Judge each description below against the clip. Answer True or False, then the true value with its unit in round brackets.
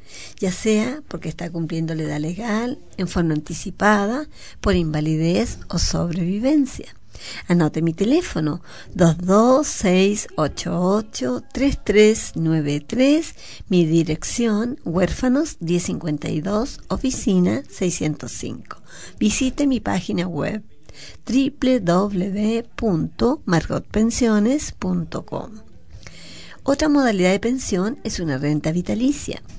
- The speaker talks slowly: True (80 wpm)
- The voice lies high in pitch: True (195 Hz)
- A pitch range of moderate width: False (5.9 semitones)